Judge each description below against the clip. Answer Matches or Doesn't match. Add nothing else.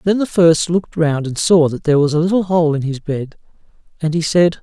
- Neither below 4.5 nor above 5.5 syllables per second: Doesn't match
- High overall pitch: Doesn't match